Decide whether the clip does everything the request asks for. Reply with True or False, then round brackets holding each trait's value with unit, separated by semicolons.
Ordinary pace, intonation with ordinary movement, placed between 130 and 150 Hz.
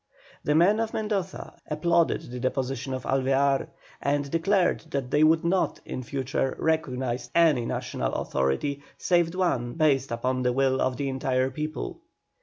True (150 wpm; 4.1 semitones; 140 Hz)